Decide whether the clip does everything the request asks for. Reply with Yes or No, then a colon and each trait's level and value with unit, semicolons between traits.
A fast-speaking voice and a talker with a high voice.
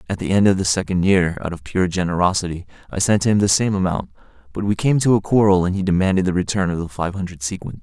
No: fast, 255 wpm; very low, 95 Hz